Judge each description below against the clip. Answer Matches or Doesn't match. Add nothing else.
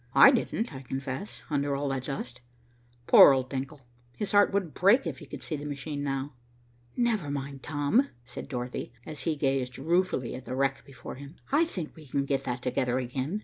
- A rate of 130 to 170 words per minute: Doesn't match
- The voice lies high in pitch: Doesn't match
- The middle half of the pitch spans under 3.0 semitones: Doesn't match